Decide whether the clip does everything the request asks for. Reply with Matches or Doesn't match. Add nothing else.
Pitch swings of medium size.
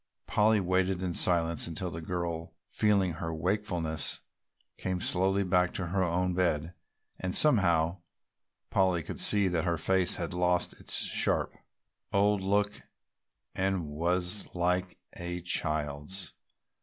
Doesn't match